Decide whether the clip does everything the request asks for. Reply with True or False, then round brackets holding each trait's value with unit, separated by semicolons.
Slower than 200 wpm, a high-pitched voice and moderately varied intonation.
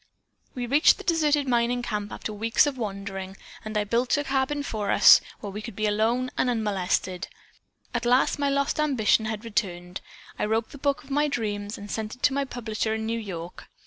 False (205 wpm; 225 Hz; 4.2 semitones)